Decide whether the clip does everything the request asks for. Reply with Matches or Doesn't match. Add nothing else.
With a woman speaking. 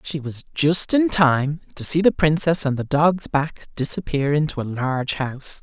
Doesn't match